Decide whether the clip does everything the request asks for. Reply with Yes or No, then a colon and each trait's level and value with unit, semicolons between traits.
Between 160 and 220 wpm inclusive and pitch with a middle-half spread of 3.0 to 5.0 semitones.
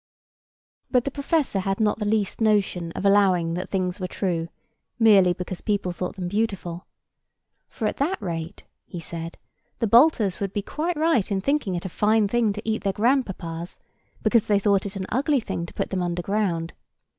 Yes: average, 185 wpm; average, 3.7 semitones